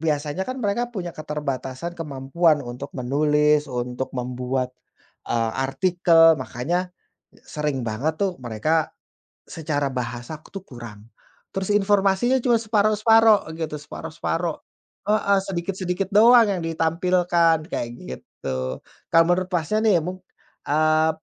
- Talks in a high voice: No, medium, 160 Hz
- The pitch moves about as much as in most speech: No, wide, 6.0 semitones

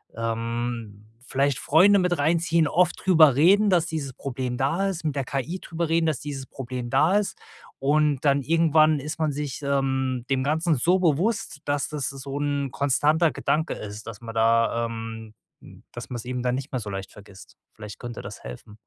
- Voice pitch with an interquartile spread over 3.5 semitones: Yes, average, 4.8 semitones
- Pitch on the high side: No, medium, 140 Hz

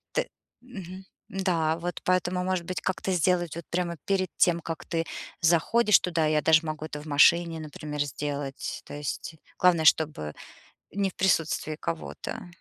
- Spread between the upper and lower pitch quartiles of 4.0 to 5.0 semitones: No, average, 3.0 semitones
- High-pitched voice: No, medium, 170 Hz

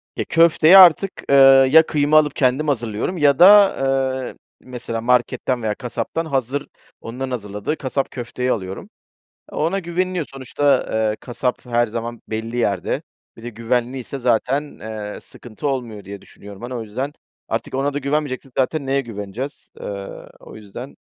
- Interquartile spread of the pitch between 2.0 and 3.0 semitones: No, average, 4.1 semitones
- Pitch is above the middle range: No, low, 130 Hz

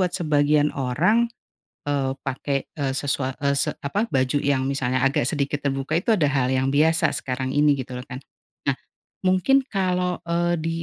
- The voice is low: No, medium, 145 Hz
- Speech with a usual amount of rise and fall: Yes, average, 4.0 semitones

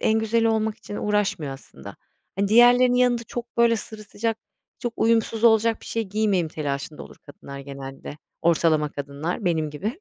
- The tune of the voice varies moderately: No, wide, 6.9 semitones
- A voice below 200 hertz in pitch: No, high, 210 Hz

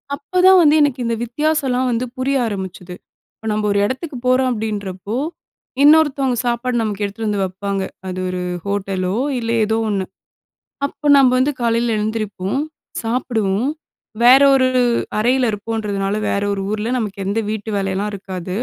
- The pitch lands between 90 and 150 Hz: No, high, 220 Hz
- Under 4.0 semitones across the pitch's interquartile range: No, average, 4.3 semitones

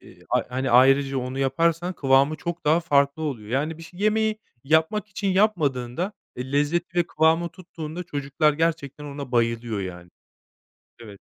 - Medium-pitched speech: Yes, medium, 150 Hz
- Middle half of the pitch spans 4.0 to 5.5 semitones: Yes, average, 4.4 semitones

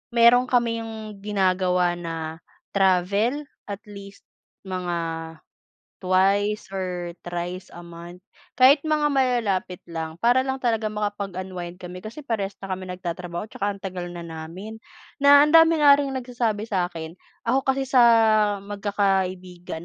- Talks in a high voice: Yes, high, 195 Hz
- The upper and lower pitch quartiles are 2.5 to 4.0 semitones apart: No, average, 4.6 semitones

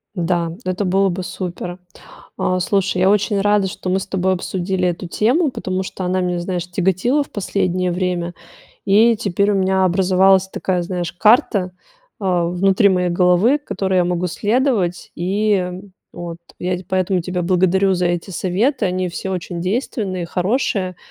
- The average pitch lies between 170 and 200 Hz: Yes, medium, 185 Hz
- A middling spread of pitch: No, narrow, 1.7 semitones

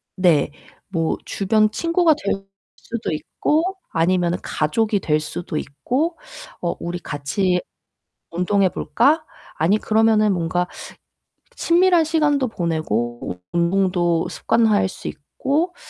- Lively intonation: Yes, wide, 5.8 semitones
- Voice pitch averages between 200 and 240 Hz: No, high, 190 Hz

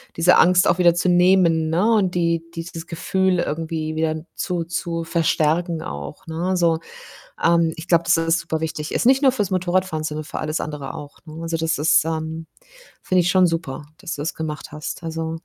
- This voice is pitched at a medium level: Yes, medium, 165 Hz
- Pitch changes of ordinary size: No, narrow, 1.9 semitones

